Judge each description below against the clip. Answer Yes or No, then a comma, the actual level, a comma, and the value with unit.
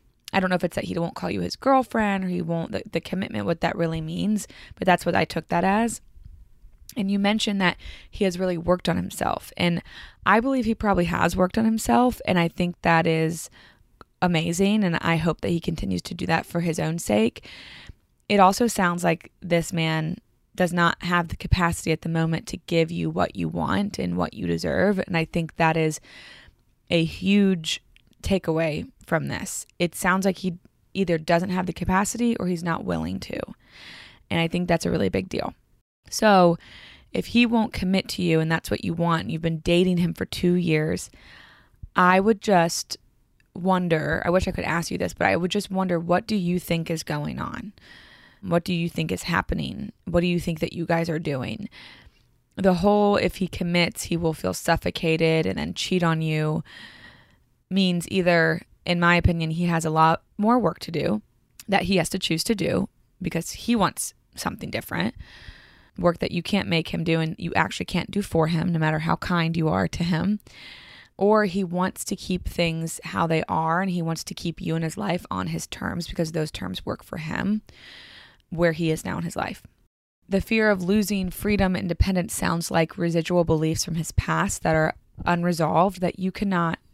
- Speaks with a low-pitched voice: No, medium, 170 Hz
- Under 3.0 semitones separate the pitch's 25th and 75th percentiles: Yes, narrow, 2.5 semitones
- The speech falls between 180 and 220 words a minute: Yes, fast, 205 wpm